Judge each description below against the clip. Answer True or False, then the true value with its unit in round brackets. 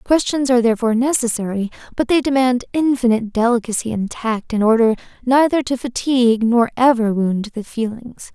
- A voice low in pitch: False (240 Hz)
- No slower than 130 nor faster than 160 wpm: True (150 wpm)